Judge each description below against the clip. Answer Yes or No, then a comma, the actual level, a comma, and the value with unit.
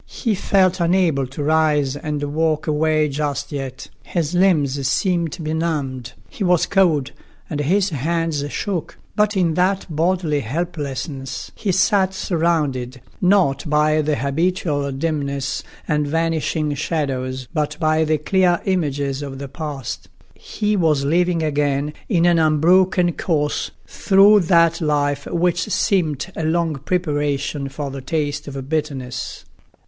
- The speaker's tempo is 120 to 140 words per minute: Yes, slow, 135 wpm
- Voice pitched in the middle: Yes, medium, 155 Hz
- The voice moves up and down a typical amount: Yes, average, 3.4 semitones